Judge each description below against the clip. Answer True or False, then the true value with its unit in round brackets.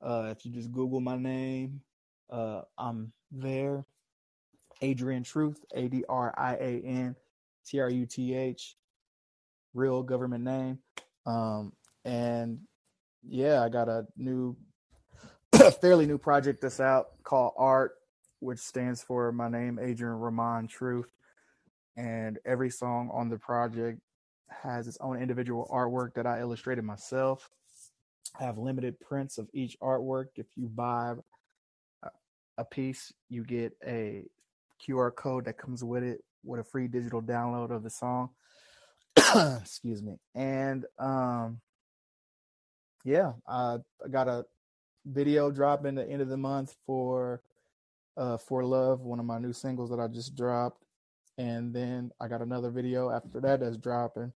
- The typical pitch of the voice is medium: False (125 Hz)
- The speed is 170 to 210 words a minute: False (145 wpm)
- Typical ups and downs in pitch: False (1.8 semitones)